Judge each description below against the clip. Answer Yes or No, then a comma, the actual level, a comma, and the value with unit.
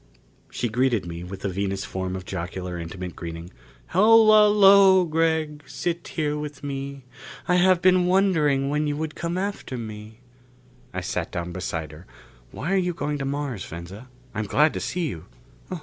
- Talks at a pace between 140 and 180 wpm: Yes, average, 170 wpm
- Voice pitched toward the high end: No, medium, 140 Hz